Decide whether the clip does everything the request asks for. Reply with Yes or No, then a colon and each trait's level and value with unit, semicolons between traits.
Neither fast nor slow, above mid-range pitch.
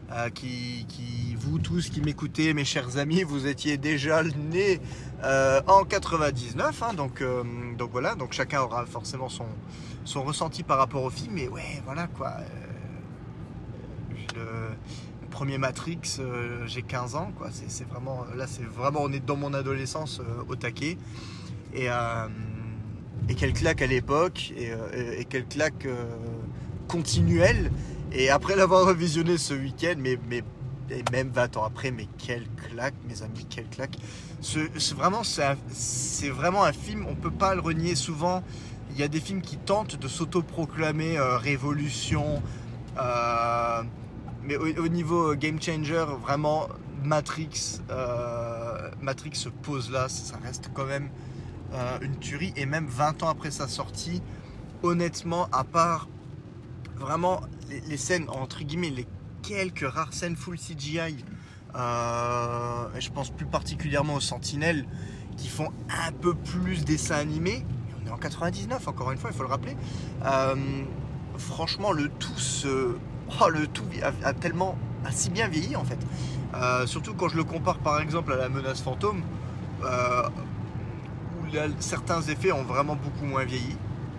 No: average, 160 wpm; low, 135 Hz